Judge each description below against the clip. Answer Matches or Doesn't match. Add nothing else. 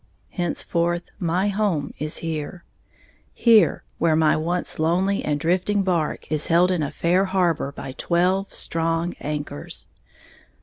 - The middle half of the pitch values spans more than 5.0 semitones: Doesn't match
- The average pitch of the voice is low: Doesn't match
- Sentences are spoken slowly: Matches